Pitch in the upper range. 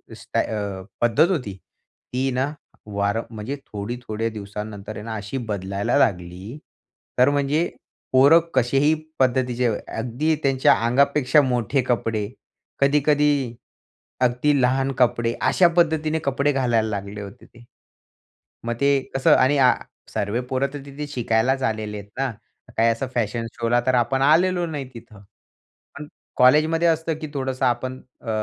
No: low, 125 Hz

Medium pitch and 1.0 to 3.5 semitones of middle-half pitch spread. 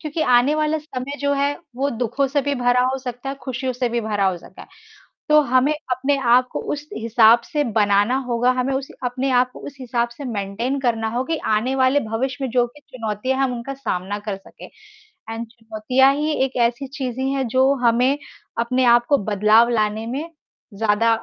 No: very high, 250 Hz; average, 2.9 semitones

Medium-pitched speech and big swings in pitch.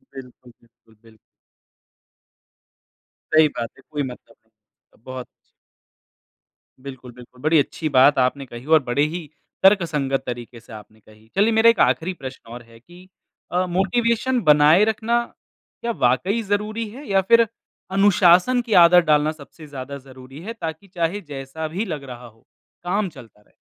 Yes: medium, 155 Hz; wide, 7.3 semitones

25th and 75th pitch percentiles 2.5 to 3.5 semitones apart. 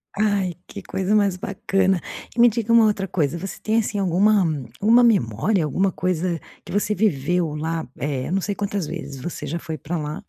No: average, 4.2 semitones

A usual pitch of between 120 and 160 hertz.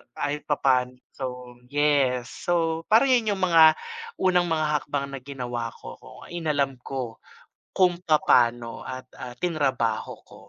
Yes: medium, 140 Hz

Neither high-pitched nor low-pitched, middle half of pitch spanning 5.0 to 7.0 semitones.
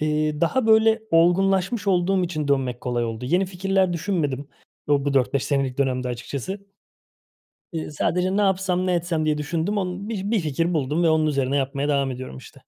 Yes: medium, 160 Hz; average, 5.3 semitones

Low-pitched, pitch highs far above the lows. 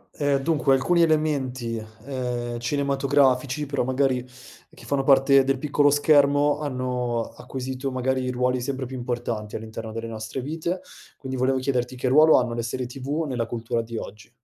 No: low, 130 Hz; narrow, 2.6 semitones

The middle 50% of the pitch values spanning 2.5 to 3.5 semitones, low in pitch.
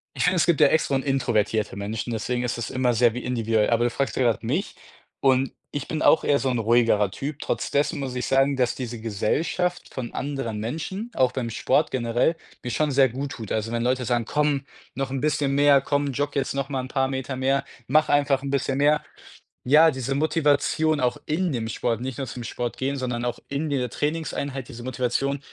Yes: average, 2.9 semitones; low, 130 Hz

